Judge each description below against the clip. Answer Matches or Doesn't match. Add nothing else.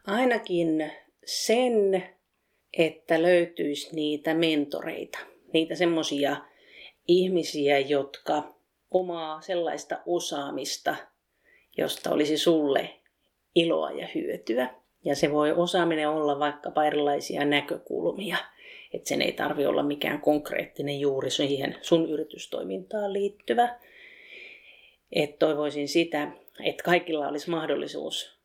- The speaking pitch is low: Doesn't match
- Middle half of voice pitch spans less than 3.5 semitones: Doesn't match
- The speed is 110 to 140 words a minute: Doesn't match